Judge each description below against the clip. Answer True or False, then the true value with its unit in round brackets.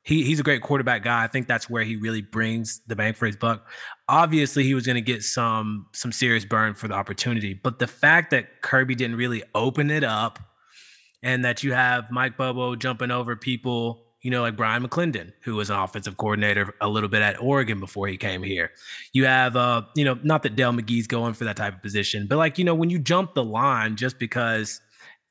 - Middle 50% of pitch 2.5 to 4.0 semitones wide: True (2.9 semitones)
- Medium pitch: False (120 Hz)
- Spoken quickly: True (225 wpm)